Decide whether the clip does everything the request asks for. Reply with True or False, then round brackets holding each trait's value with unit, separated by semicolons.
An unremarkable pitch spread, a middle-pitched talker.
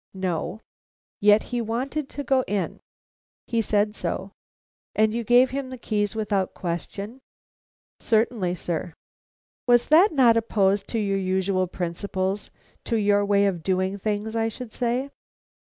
False (3.5 semitones; 210 Hz)